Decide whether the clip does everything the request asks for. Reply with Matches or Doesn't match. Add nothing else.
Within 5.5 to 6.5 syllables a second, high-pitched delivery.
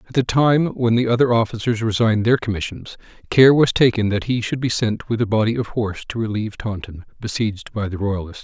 Doesn't match